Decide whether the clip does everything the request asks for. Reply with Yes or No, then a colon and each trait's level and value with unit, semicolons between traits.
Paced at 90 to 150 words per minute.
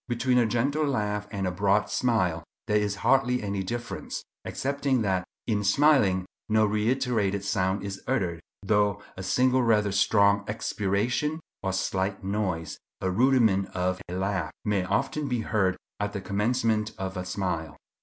Yes: average, 145 wpm